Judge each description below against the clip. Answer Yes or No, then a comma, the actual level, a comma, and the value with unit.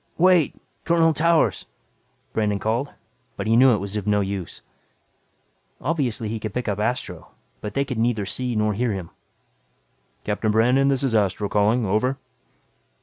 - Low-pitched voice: Yes, low, 110 Hz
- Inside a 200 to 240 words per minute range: No, average, 150 wpm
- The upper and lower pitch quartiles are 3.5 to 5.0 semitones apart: Yes, average, 4.2 semitones